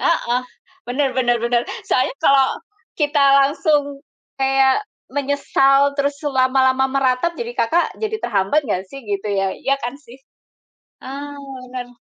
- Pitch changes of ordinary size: No, narrow, 2.3 semitones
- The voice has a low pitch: No, very high, 270 Hz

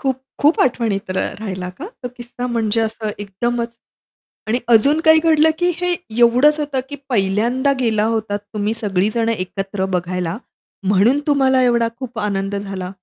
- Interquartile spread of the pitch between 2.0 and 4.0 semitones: No, average, 4.6 semitones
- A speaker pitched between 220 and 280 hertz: Yes, high, 230 Hz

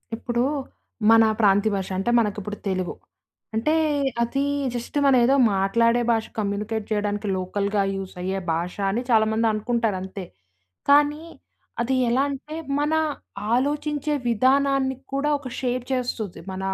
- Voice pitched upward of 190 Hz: Yes, high, 225 Hz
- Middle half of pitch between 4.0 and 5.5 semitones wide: Yes, average, 4.7 semitones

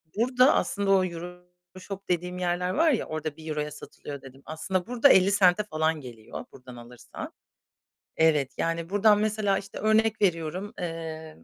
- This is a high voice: No, medium, 180 Hz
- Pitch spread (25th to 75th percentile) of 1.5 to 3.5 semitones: No, average, 4.3 semitones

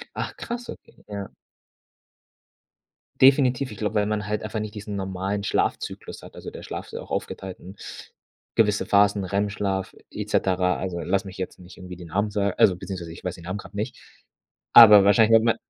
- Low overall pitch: Yes, low, 100 Hz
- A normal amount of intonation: No, narrow, 2.2 semitones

